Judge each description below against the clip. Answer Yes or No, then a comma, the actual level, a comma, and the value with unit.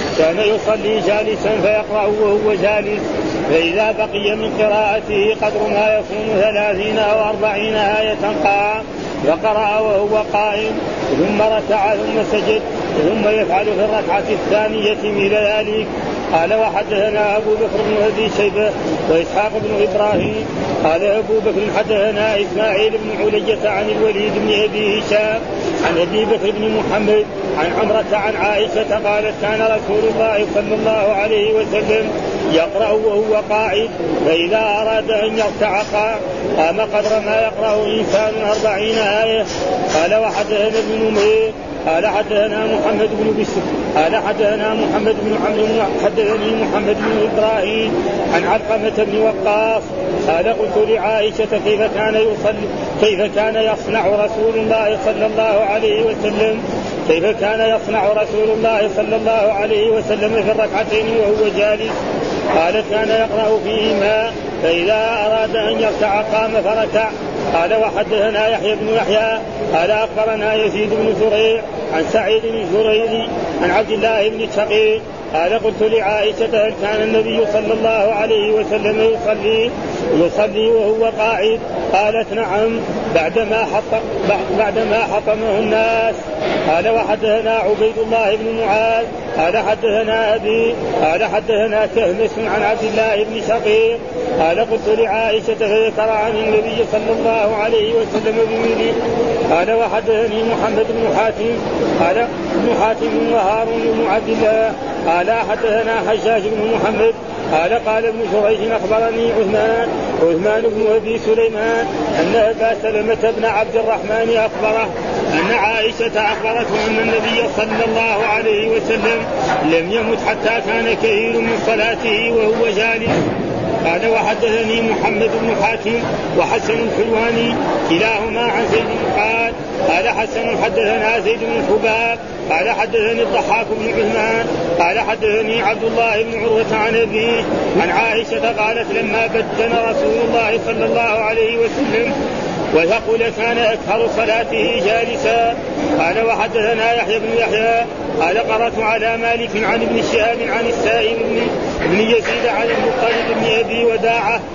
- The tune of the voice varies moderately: No, narrow, 0.9 semitones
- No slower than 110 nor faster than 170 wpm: Yes, average, 130 wpm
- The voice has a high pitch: Yes, high, 215 Hz